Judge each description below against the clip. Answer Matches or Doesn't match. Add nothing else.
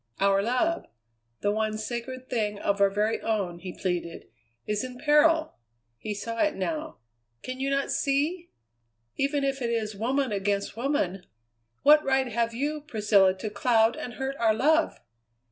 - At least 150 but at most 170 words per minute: Matches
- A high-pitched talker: Matches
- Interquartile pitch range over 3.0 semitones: Matches